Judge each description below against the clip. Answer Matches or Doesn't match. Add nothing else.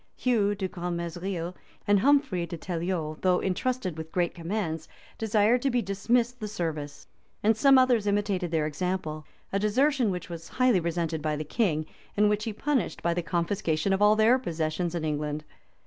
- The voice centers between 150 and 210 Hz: Matches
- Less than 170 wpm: Doesn't match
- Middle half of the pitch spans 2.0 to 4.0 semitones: Doesn't match